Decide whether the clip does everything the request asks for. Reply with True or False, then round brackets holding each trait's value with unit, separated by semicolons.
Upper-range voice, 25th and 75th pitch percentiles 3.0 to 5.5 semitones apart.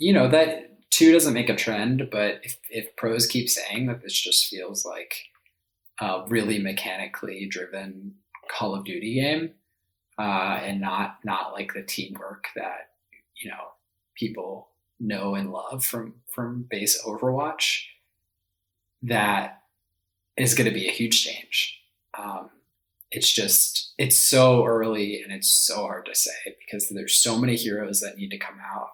False (105 Hz; 3.8 semitones)